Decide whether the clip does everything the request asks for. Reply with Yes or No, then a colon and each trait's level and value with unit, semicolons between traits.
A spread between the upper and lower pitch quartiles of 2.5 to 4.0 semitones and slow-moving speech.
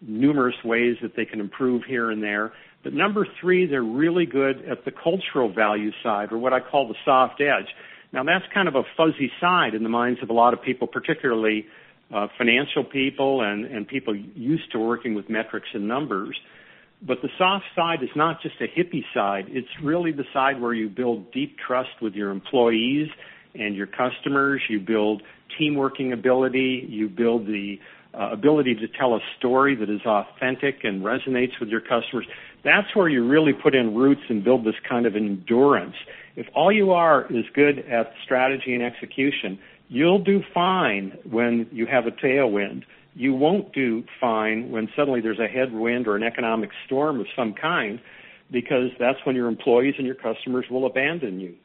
No: average, 3.7 semitones; average, 185 wpm